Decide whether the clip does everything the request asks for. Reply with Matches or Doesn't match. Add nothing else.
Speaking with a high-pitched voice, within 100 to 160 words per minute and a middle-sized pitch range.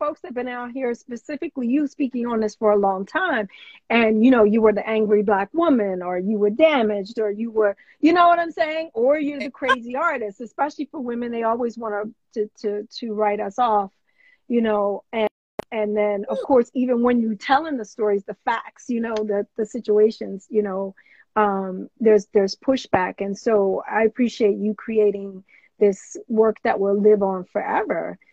Doesn't match